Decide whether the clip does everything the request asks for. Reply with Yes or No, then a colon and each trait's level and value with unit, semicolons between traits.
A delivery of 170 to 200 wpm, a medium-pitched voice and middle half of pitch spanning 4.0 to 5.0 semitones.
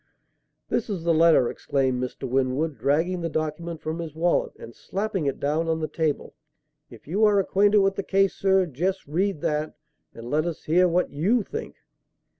Yes: average, 185 wpm; medium, 165 Hz; average, 4.4 semitones